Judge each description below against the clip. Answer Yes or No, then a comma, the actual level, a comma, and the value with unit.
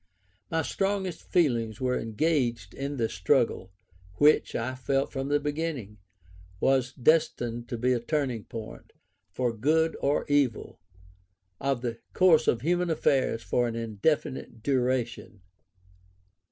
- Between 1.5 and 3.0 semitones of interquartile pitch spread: No, average, 4.3 semitones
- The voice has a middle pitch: No, low, 130 Hz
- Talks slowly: Yes, slow, 125 wpm